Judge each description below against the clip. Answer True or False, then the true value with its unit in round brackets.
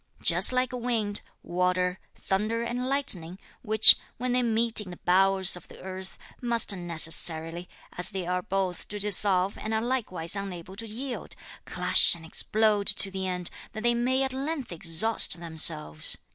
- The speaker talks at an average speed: True (160 wpm)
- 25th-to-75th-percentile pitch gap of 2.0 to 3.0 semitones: False (4.6 semitones)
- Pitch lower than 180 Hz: False (195 Hz)